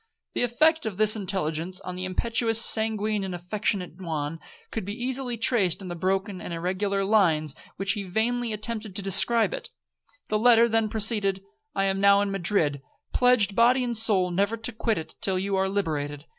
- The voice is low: No, high, 200 Hz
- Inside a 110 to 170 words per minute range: No, average, 185 wpm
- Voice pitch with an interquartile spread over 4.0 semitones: No, average, 3.5 semitones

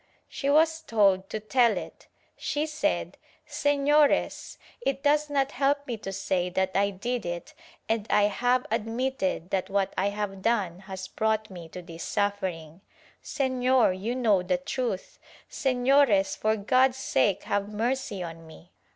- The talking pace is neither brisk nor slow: Yes, average, 160 wpm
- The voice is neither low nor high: No, high, 215 Hz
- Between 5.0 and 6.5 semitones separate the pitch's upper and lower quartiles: Yes, wide, 5.6 semitones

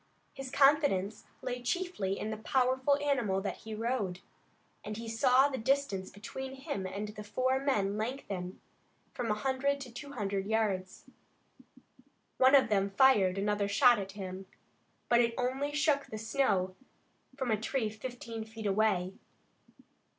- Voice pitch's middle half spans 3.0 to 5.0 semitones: Yes, average, 4.7 semitones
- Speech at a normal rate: Yes, average, 150 wpm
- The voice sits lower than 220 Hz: No, high, 225 Hz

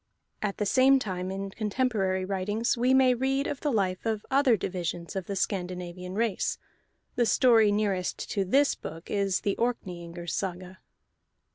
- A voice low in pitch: No, high, 200 Hz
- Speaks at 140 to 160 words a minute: Yes, average, 155 wpm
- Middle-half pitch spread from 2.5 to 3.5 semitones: No, average, 4.3 semitones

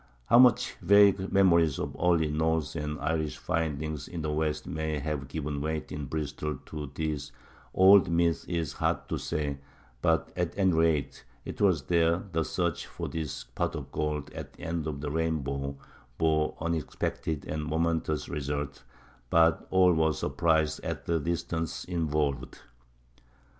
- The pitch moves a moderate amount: No, narrow, 1.9 semitones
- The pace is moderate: Yes, average, 155 wpm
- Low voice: Yes, very low, 80 Hz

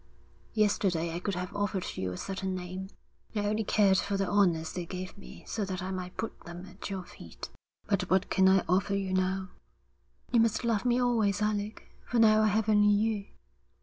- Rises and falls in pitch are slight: Yes, narrow, 2.3 semitones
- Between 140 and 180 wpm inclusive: No, average, 200 wpm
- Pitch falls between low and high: No, high, 195 Hz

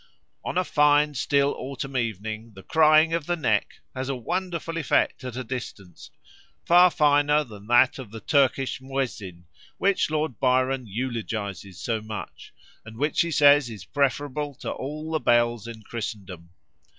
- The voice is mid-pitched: No, low, 130 Hz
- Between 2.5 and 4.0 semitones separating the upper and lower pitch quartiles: No, average, 4.9 semitones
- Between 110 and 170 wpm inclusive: Yes, average, 155 wpm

